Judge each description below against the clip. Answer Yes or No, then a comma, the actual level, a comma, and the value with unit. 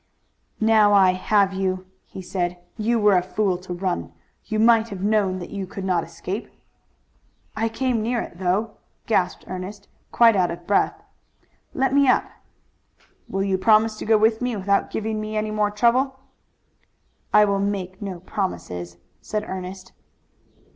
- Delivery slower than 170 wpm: Yes, average, 160 wpm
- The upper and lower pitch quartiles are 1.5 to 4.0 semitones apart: Yes, average, 2.9 semitones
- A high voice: Yes, high, 200 Hz